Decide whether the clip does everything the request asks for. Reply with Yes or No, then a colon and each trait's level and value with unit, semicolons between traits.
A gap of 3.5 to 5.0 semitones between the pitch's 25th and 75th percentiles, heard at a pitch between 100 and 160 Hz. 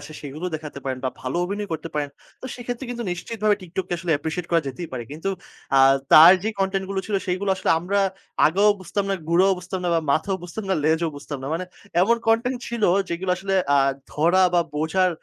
No: average, 3.9 semitones; medium, 180 Hz